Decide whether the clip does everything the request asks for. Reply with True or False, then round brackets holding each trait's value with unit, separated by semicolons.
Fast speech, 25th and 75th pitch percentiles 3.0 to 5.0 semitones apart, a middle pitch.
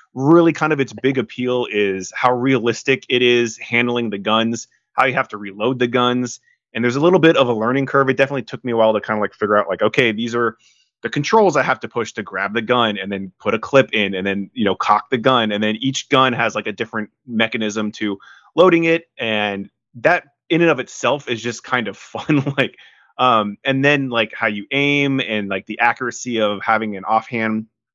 False (230 wpm; 3.6 semitones; 120 Hz)